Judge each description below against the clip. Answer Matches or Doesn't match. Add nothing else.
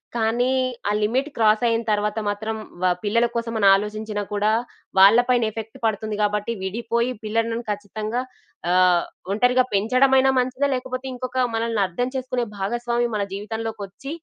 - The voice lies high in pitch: Matches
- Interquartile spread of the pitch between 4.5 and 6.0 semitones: Doesn't match